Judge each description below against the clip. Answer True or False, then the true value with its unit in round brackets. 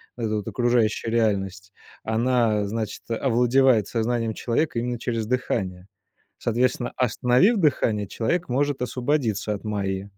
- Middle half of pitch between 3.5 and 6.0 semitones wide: False (2.8 semitones)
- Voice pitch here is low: True (115 Hz)